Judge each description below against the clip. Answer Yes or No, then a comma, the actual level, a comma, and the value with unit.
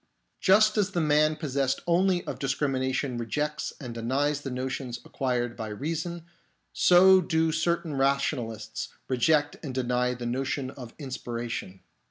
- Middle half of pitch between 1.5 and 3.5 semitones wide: No, average, 4.4 semitones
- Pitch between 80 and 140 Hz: Yes, low, 135 Hz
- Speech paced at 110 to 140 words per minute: Yes, slow, 135 wpm